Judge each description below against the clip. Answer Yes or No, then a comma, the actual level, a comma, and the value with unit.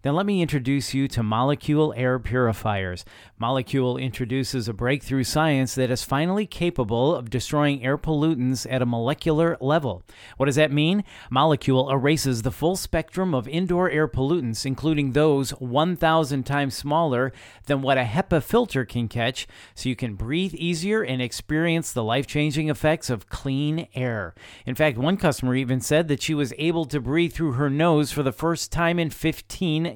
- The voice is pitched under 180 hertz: Yes, medium, 140 Hz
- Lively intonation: No, average, 3.8 semitones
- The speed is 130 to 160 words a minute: No, average, 175 wpm